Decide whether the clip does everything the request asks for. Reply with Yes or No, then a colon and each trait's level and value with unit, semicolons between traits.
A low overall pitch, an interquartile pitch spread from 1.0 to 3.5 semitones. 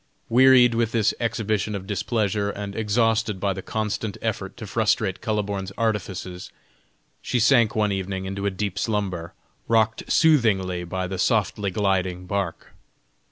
Yes: low, 105 Hz; average, 2.7 semitones